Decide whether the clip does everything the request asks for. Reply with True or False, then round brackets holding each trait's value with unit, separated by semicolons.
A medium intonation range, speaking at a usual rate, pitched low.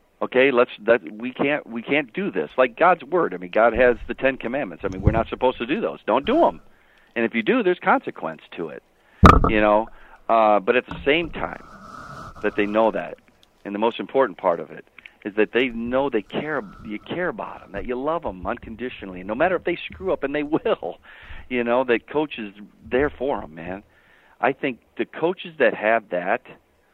False (3.6 semitones; 215 wpm; 115 Hz)